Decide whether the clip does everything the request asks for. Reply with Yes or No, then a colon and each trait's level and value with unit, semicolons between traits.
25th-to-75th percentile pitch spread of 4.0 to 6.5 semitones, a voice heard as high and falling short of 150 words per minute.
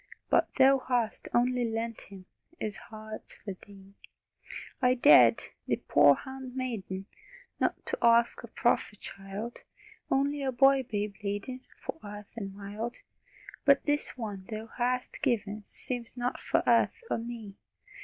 No: average, 3.6 semitones; high, 235 Hz; average, 140 wpm